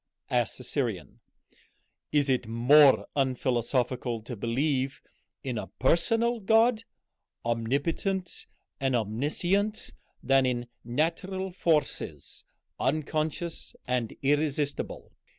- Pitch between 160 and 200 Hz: No, medium, 140 Hz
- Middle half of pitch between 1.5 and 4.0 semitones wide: No, average, 5.3 semitones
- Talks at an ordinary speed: No, slow, 90 wpm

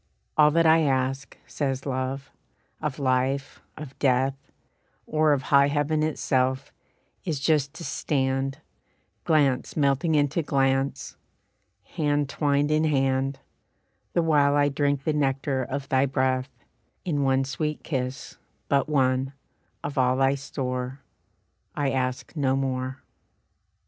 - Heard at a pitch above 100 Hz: Yes, low, 135 Hz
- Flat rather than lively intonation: Yes, narrow, 1.8 semitones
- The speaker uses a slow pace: Yes, slow, 125 wpm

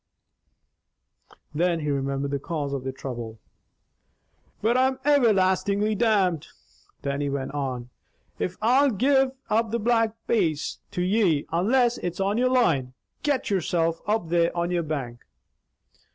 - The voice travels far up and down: Yes, wide, 7.9 semitones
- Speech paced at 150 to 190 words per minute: No, slow, 135 wpm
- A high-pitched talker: No, medium, 180 Hz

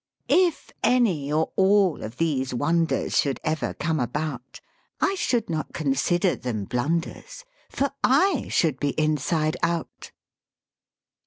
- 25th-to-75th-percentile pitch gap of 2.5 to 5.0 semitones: No, wide, 5.4 semitones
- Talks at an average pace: No, slow, 125 wpm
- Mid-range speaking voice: Yes, medium, 160 Hz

